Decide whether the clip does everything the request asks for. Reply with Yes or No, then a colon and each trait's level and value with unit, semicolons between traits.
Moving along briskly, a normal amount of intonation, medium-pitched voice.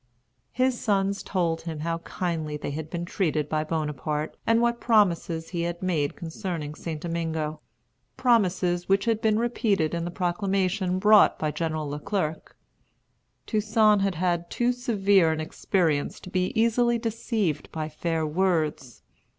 No: average, 150 wpm; average, 4.6 semitones; medium, 175 Hz